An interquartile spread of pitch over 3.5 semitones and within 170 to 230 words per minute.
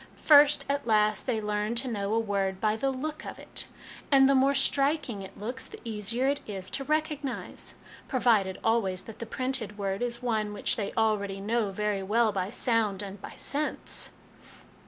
Yes: average, 4.4 semitones; average, 180 wpm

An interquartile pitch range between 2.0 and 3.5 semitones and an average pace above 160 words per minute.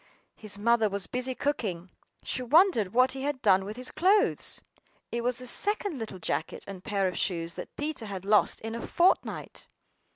No: average, 5.2 semitones; average, 185 wpm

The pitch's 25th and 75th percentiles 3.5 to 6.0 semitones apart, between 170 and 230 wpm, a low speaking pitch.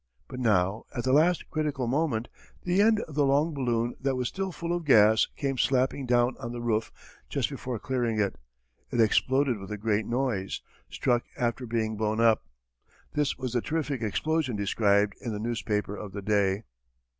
Yes: average, 4.2 semitones; average, 180 wpm; low, 120 Hz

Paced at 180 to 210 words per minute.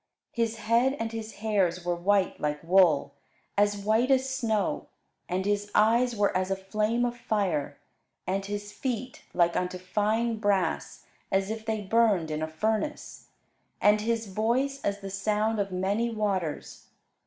No: average, 155 wpm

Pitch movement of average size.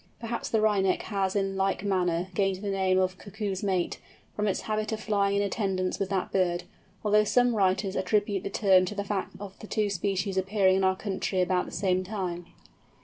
No: narrow, 1.8 semitones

